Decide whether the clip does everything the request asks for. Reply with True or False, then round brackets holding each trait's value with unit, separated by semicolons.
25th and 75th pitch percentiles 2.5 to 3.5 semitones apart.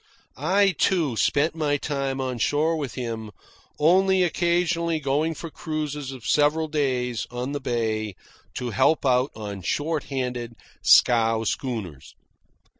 False (4.7 semitones)